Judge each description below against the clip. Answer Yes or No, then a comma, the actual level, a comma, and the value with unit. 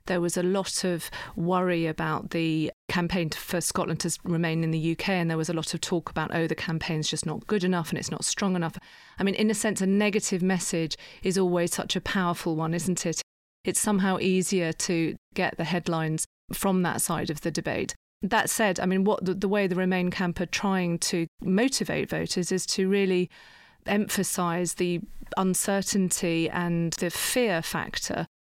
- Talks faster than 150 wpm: Yes, average, 190 wpm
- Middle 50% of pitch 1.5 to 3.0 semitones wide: Yes, narrow, 2.4 semitones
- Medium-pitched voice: Yes, medium, 180 Hz